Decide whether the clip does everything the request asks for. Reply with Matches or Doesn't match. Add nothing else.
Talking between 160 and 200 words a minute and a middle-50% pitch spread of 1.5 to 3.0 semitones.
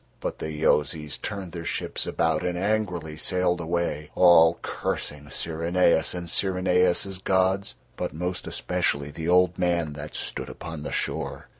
Doesn't match